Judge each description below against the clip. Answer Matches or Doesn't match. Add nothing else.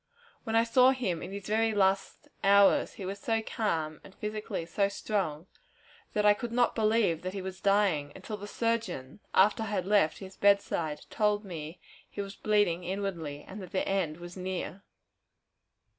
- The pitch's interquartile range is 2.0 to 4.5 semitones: Matches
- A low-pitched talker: Doesn't match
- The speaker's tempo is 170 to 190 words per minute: Matches